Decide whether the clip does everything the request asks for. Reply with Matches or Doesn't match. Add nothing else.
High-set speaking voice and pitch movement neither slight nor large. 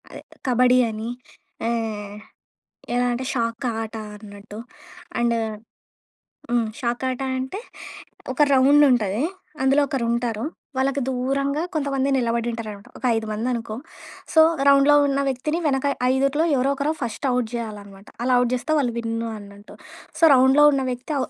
Matches